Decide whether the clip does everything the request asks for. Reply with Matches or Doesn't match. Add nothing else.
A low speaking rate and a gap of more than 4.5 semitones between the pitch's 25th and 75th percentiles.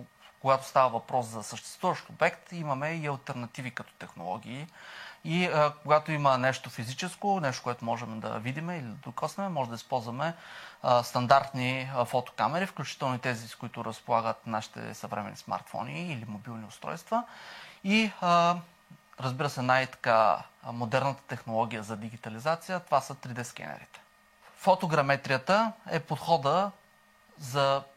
Doesn't match